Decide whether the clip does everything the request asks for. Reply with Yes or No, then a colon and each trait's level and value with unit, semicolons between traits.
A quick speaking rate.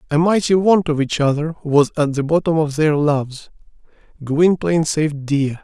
No: average, 170 wpm